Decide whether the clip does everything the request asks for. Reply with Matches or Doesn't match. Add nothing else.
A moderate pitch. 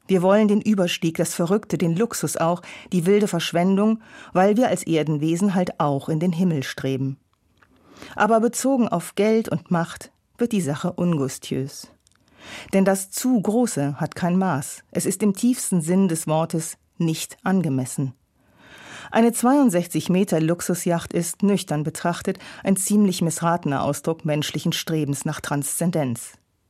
Matches